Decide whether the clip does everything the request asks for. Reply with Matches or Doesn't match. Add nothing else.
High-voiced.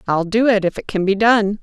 Matches